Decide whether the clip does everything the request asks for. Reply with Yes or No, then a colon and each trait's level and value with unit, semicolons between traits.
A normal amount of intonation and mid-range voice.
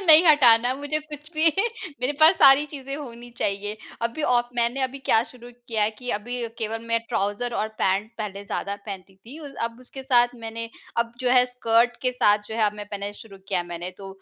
No: average, 3.8 semitones; high, 235 Hz